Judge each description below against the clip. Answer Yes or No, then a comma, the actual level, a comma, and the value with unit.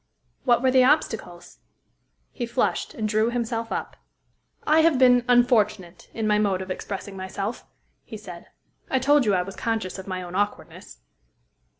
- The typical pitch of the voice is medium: No, high, 220 Hz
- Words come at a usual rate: Yes, average, 165 wpm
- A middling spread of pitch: Yes, average, 4.3 semitones